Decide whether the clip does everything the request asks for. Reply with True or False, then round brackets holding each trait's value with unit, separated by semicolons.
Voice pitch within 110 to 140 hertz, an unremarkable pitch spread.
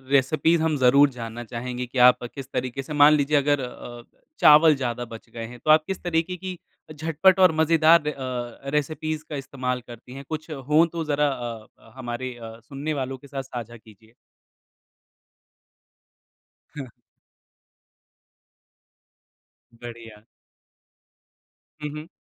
True (135 Hz; 4.0 semitones)